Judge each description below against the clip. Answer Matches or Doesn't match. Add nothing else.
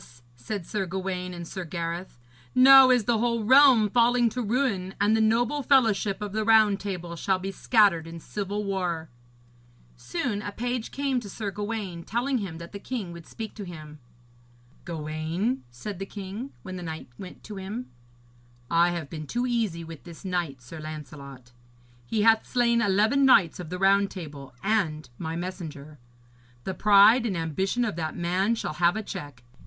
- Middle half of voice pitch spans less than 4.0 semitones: Doesn't match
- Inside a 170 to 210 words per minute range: Matches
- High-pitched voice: Matches